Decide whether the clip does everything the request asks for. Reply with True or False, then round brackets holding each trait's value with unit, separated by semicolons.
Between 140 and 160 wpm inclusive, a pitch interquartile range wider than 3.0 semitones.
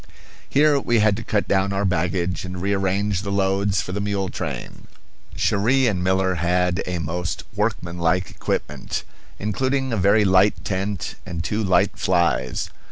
False (155 wpm; 2.4 semitones)